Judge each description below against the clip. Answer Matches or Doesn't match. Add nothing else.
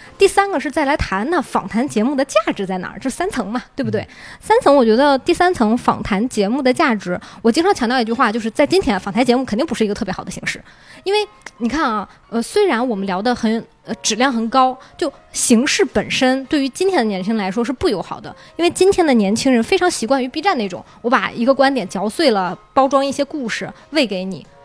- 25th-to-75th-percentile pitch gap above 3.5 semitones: Matches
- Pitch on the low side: Doesn't match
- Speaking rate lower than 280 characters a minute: Doesn't match